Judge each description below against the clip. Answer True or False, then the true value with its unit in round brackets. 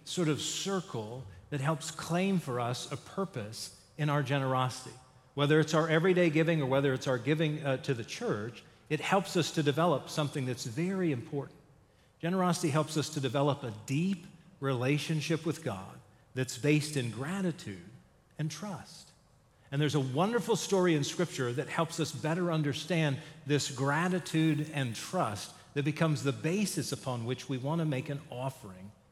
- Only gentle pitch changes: False (3.7 semitones)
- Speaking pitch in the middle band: True (150 Hz)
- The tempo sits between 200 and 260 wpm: False (165 wpm)